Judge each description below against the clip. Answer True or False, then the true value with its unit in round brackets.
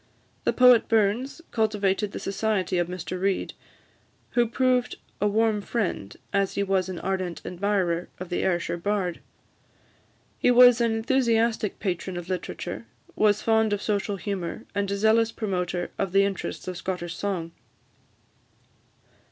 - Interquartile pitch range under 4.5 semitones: True (3.3 semitones)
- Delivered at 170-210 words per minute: False (145 wpm)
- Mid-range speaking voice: False (200 Hz)